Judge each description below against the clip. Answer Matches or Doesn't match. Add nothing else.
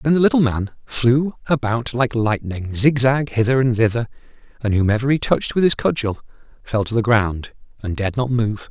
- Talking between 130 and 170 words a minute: Doesn't match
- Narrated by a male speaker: Matches